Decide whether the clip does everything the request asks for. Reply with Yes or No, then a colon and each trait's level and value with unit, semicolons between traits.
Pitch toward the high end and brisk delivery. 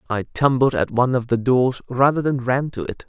No: low, 125 Hz; fast, 235 wpm